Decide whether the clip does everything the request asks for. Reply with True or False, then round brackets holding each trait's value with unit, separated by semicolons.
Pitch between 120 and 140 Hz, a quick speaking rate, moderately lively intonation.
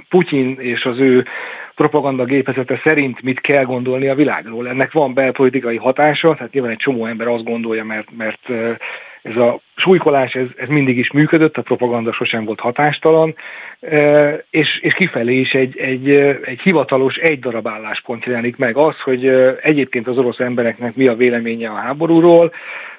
True (130 Hz; 160 wpm; 3.4 semitones)